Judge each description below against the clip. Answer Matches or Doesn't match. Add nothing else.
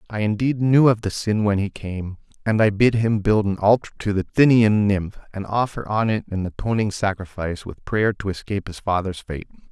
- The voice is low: Matches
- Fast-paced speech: Matches